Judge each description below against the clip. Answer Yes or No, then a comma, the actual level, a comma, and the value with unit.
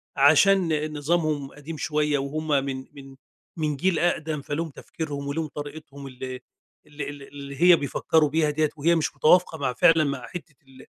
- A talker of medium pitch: Yes, medium, 150 Hz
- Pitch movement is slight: Yes, narrow, 2.2 semitones